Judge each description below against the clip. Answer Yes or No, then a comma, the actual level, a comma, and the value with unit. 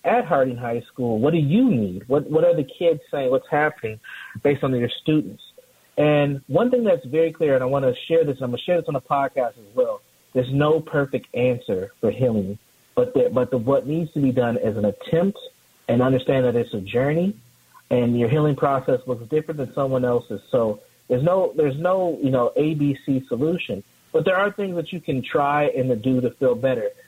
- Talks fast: Yes, fast, 220 wpm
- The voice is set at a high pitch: No, medium, 140 Hz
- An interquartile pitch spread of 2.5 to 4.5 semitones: No, average, 5.0 semitones